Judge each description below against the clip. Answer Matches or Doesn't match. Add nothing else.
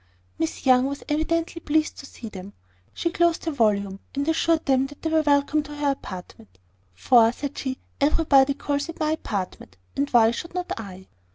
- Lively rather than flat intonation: Matches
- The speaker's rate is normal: Matches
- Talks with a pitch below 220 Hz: Doesn't match